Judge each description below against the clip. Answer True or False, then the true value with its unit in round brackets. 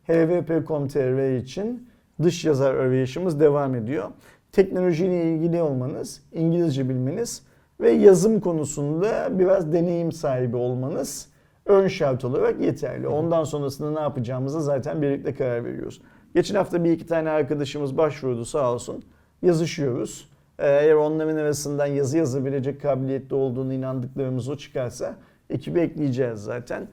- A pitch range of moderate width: True (3.8 semitones)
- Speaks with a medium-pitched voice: True (150 Hz)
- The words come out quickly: False (120 wpm)